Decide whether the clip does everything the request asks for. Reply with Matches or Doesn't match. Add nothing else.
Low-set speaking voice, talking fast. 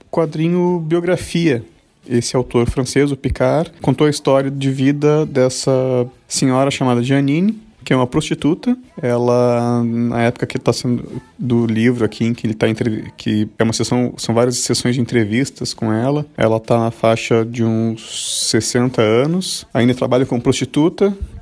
Doesn't match